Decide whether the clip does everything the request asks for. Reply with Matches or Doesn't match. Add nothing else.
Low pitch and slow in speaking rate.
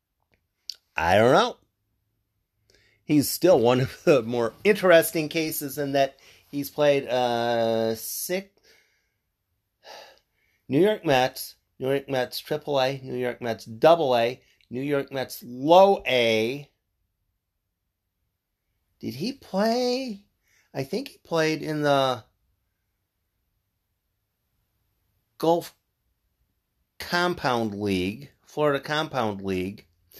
Matches